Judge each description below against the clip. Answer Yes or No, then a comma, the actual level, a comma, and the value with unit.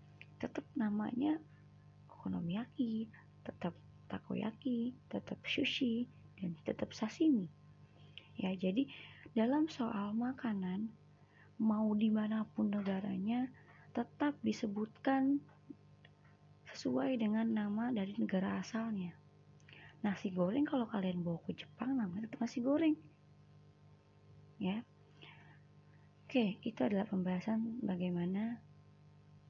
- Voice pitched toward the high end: Yes, high, 215 Hz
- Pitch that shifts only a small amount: No, average, 5.1 semitones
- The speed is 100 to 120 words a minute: No, slow, 85 wpm